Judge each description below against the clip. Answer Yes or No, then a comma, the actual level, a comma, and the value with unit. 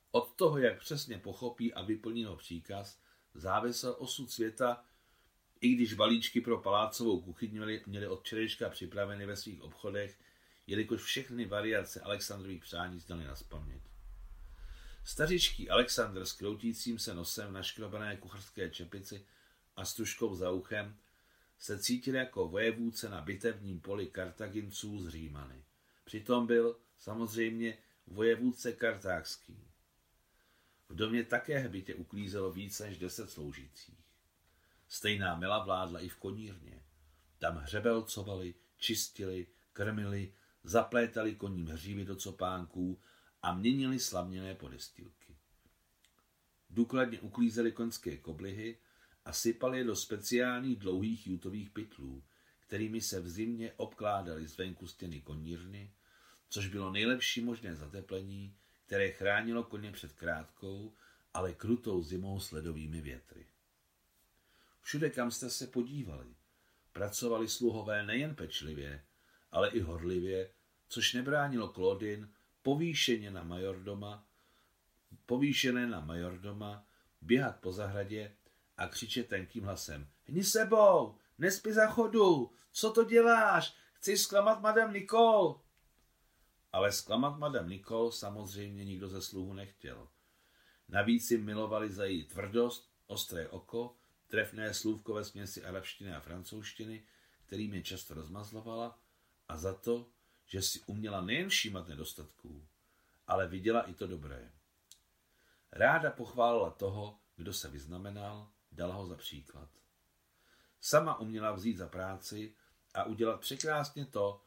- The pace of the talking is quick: No, average, 120 wpm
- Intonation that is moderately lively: Yes, average, 4.4 semitones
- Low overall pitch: Yes, low, 100 Hz